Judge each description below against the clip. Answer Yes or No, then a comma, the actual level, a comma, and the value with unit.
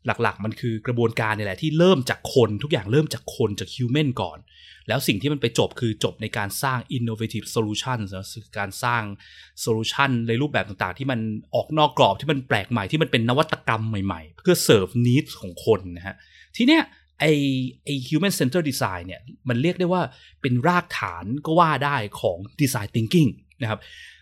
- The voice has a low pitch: Yes, low, 120 Hz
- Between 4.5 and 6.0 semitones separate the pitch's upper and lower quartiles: Yes, average, 5.2 semitones